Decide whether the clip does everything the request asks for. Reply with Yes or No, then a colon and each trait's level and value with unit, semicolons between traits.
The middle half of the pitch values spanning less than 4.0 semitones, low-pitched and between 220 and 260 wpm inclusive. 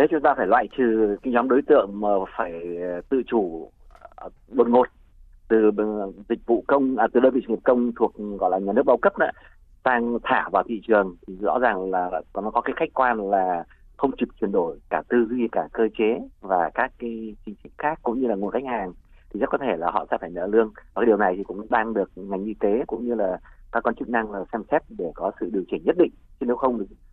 Yes: average, 3.2 semitones; low, 115 Hz; fast, 250 wpm